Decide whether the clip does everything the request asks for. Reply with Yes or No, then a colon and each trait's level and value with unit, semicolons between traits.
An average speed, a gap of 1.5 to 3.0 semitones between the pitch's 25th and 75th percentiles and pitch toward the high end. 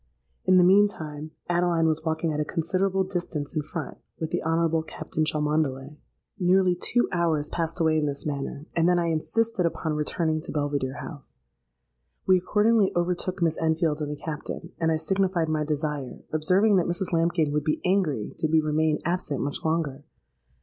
No: average, 175 wpm; average, 2.7 semitones; medium, 160 Hz